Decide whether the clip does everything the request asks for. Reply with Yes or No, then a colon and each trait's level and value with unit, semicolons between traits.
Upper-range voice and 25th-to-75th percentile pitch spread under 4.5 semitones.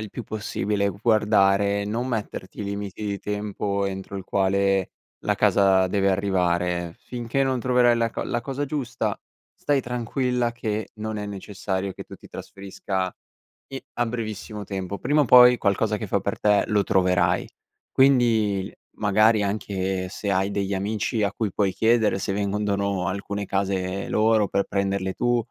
No: low, 100 Hz; narrow, 2.5 semitones